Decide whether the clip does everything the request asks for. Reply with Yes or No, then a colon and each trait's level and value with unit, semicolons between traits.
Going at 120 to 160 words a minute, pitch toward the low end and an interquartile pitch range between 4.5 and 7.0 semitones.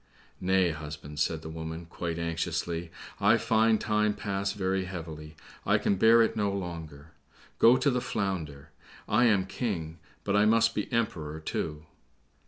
Yes: average, 150 wpm; very low, 90 Hz; average, 4.9 semitones